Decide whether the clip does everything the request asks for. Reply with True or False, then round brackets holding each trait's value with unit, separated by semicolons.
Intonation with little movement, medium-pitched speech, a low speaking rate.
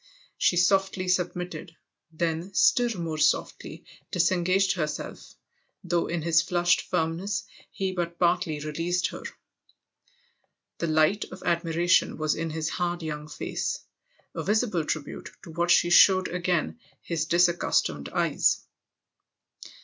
True (2.0 semitones; 175 Hz; 125 wpm)